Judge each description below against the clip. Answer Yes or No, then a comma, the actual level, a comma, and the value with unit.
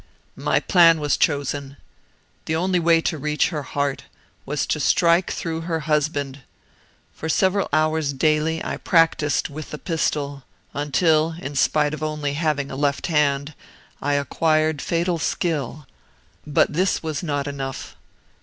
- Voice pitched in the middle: Yes, medium, 155 Hz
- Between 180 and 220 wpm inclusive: No, average, 145 wpm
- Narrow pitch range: Yes, narrow, 2.3 semitones